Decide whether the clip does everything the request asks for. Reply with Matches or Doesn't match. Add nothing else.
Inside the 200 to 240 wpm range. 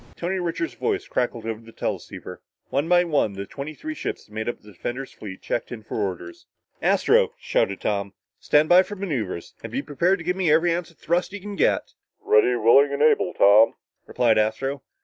Matches